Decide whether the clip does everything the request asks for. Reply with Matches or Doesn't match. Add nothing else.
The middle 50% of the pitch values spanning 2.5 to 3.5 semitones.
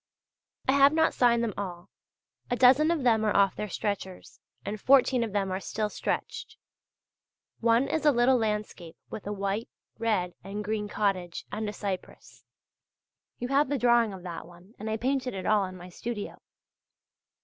Doesn't match